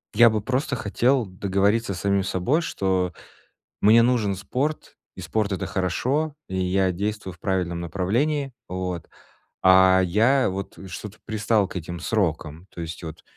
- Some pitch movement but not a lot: Yes, average, 4.0 semitones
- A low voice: Yes, low, 100 Hz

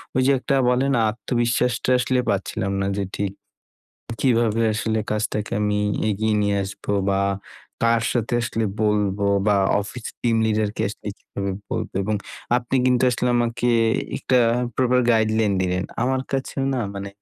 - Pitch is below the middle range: Yes, low, 110 Hz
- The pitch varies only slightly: No, average, 3.1 semitones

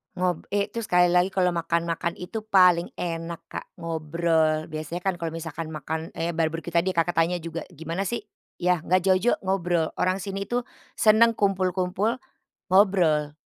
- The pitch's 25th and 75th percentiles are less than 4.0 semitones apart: Yes, narrow, 2.4 semitones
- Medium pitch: Yes, medium, 175 Hz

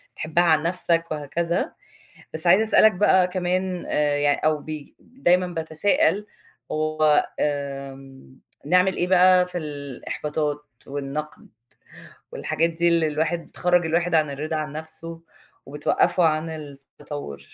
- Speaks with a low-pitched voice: No, medium, 160 Hz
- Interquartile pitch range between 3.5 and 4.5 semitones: No, average, 3.1 semitones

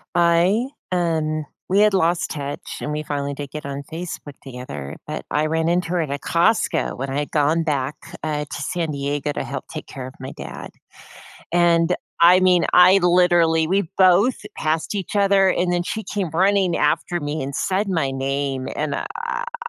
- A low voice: No, medium, 165 Hz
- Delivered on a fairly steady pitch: No, average, 3.9 semitones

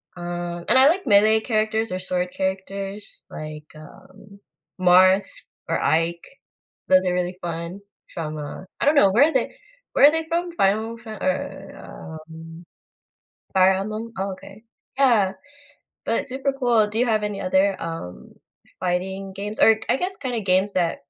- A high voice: Yes, high, 195 Hz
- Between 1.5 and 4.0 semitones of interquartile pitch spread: Yes, average, 3.6 semitones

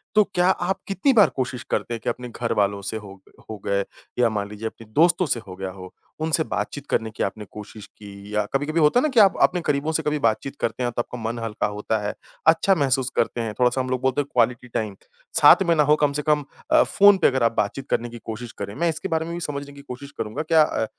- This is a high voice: No, low, 130 Hz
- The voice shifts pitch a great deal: Yes, wide, 5.9 semitones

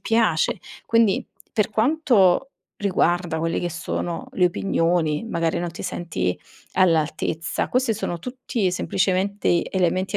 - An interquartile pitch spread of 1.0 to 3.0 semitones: No, average, 4.1 semitones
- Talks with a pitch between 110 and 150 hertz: No, medium, 180 Hz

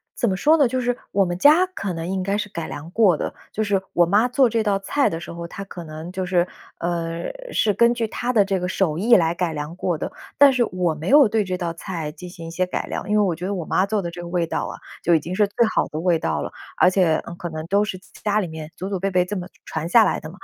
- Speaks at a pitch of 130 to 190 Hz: Yes, medium, 185 Hz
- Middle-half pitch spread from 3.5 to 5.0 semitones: Yes, average, 3.8 semitones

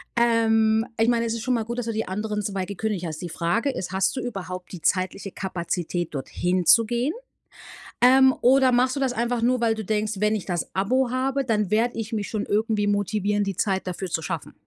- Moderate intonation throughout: Yes, average, 3.8 semitones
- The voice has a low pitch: No, high, 215 Hz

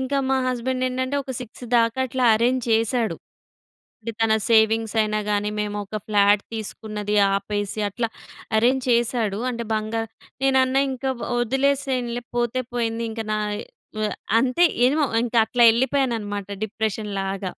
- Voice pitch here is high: Yes, high, 230 Hz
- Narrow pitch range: No, average, 3.2 semitones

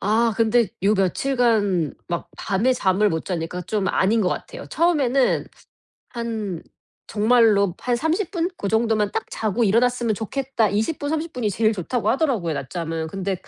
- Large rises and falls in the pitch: No, average, 4.3 semitones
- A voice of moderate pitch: No, high, 220 Hz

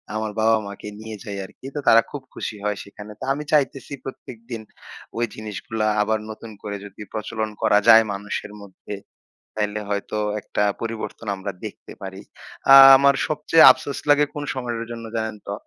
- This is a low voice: Yes, low, 110 Hz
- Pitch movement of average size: No, narrow, 2.2 semitones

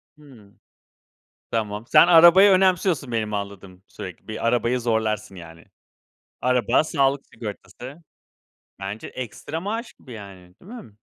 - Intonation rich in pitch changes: Yes, wide, 6.9 semitones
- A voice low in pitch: Yes, low, 115 Hz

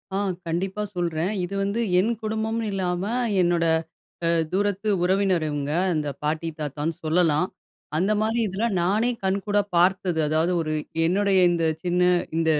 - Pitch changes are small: No, average, 3.4 semitones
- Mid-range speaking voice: Yes, medium, 180 Hz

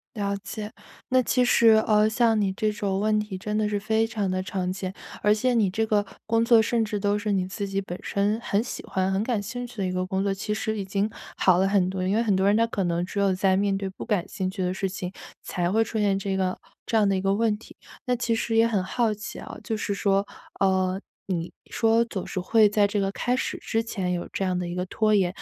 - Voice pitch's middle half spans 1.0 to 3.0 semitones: Yes, narrow, 2.4 semitones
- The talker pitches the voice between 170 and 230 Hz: Yes, high, 200 Hz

